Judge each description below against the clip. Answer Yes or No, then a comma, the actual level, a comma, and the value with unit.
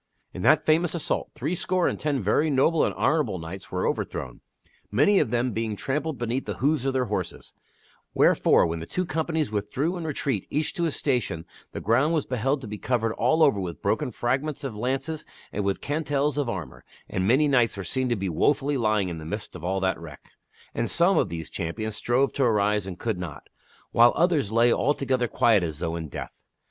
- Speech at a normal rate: No, fast, 210 wpm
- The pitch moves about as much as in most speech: No, wide, 6.6 semitones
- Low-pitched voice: Yes, low, 120 Hz